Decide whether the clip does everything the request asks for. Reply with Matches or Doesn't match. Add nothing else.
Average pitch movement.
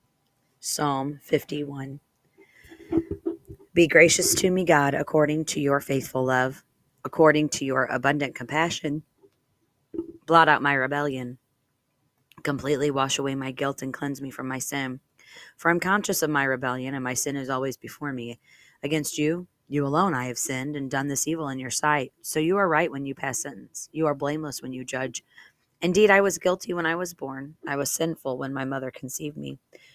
Matches